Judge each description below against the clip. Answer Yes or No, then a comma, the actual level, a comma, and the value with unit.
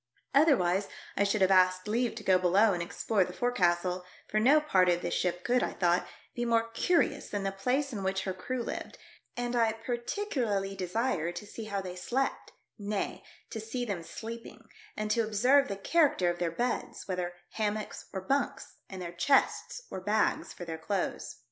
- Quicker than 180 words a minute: Yes, average, 190 wpm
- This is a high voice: Yes, high, 205 Hz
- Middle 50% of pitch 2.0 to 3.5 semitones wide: No, average, 4.7 semitones